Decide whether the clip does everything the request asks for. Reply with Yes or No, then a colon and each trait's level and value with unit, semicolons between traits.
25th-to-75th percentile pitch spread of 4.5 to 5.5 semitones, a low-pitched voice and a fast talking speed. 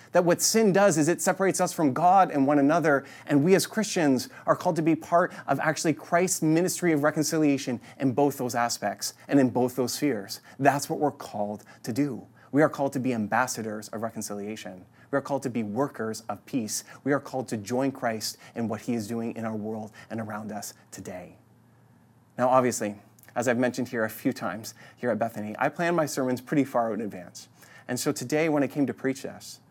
Yes: average, 4.8 semitones; low, 130 Hz; fast, 215 wpm